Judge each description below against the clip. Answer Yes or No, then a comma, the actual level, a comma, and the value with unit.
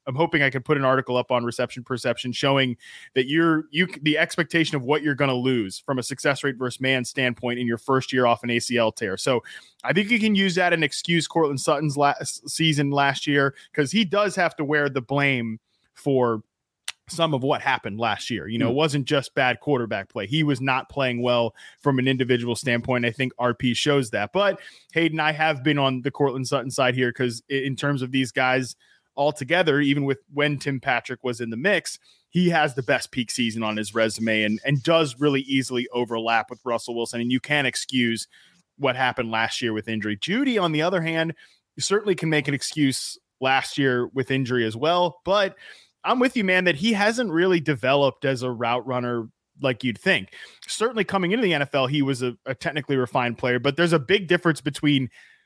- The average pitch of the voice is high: No, low, 135 Hz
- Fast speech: Yes, fast, 210 wpm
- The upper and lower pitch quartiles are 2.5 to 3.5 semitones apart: No, average, 4.0 semitones